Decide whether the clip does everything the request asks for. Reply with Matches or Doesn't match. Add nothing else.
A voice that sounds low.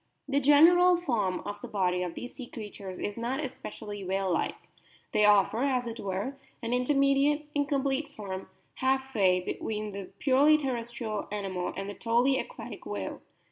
Doesn't match